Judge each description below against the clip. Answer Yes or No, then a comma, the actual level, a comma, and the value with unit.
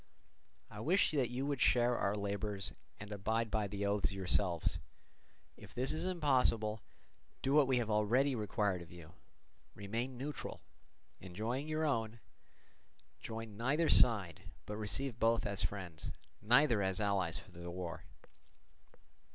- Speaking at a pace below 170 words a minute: Yes, average, 140 wpm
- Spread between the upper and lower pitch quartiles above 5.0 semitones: No, average, 4.3 semitones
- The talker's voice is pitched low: Yes, low, 110 Hz